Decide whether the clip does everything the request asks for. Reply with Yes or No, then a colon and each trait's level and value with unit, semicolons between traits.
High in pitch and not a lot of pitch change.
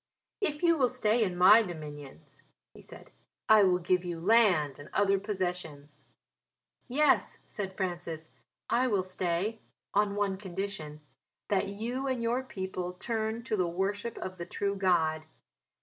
No: high, 195 Hz; average, 3.9 semitones